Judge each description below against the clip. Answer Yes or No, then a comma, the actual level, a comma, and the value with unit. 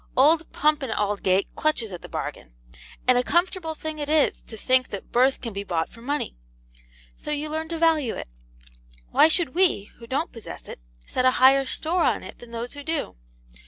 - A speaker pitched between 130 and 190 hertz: No, very high, 270 Hz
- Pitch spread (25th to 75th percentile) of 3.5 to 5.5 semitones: Yes, average, 5.2 semitones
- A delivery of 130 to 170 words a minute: No, average, 200 wpm